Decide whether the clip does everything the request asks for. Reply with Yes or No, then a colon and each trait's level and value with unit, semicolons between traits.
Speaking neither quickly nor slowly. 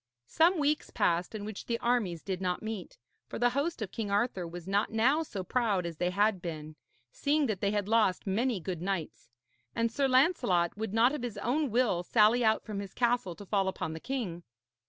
No: fast, 210 wpm